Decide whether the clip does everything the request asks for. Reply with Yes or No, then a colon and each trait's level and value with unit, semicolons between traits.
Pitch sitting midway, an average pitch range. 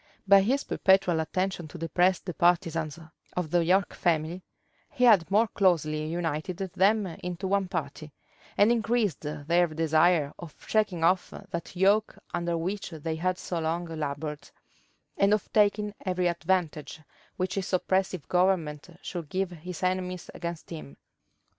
Yes: medium, 175 Hz; average, 3.0 semitones